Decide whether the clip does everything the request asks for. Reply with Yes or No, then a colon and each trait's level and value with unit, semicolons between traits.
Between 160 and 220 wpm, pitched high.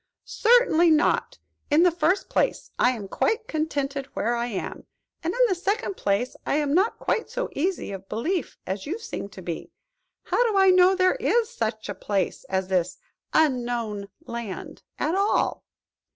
Yes: average, 170 wpm; very high, 300 Hz